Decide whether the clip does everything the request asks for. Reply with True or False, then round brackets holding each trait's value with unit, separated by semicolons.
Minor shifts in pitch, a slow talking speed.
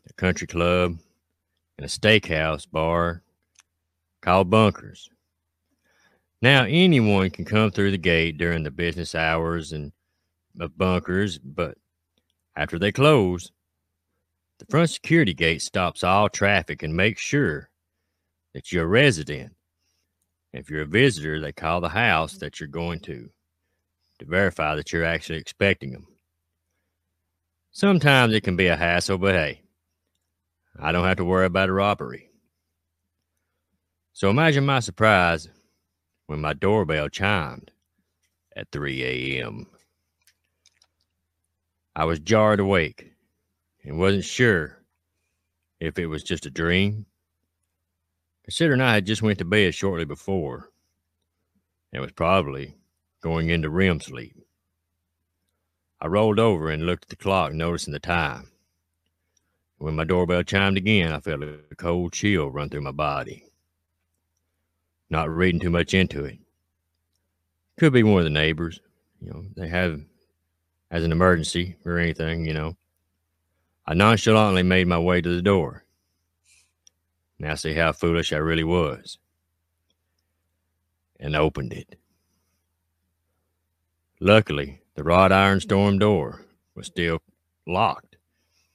True (1.9 semitones; 130 wpm)